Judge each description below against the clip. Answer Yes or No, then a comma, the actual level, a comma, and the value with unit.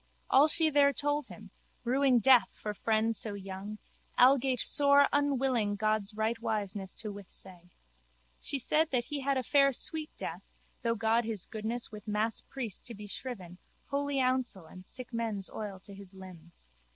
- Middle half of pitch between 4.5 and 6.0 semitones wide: Yes, average, 4.8 semitones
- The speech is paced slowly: No, average, 160 wpm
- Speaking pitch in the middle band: No, high, 230 Hz